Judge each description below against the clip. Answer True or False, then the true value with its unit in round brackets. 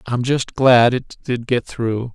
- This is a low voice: True (120 Hz)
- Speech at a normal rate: True (195 wpm)